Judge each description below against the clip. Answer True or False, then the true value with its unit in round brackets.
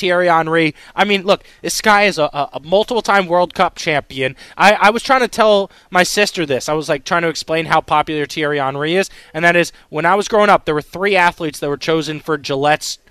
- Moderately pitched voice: True (165 Hz)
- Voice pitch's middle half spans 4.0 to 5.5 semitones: True (4.4 semitones)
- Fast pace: True (240 wpm)